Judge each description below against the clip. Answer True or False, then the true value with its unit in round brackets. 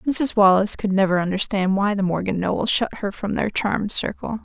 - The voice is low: False (200 Hz)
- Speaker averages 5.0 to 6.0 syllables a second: True (5.6 syllables/s)